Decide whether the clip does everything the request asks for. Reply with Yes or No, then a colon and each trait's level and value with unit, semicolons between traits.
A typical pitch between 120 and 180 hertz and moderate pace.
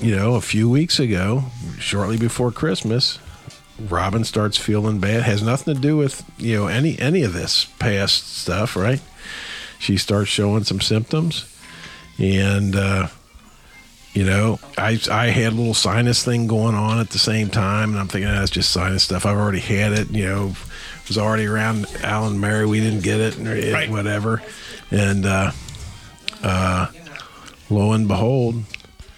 No: low, 105 Hz; average, 170 wpm